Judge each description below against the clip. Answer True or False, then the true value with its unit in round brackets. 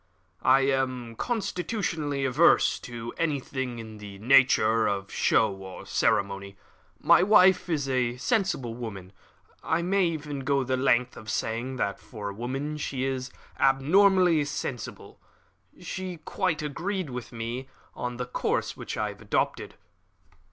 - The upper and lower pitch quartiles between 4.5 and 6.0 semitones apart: True (5.1 semitones)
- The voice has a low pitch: True (130 Hz)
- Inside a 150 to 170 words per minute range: False (135 wpm)